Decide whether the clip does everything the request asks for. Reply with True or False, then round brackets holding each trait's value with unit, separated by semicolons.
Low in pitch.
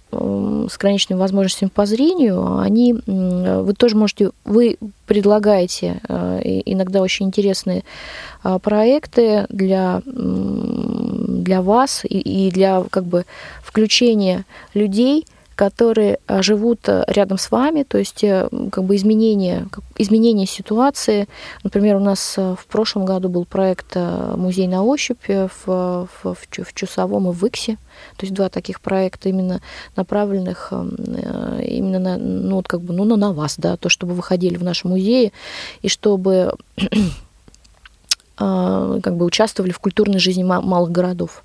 False (195 Hz)